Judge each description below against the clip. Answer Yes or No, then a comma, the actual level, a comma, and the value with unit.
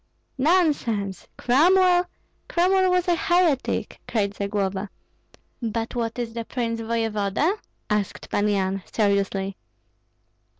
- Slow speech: Yes, slow, 100 wpm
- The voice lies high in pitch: Yes, high, 230 Hz